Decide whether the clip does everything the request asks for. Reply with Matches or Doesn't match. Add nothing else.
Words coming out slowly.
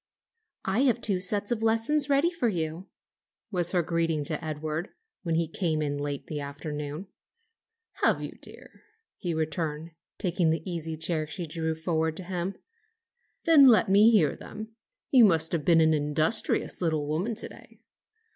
Doesn't match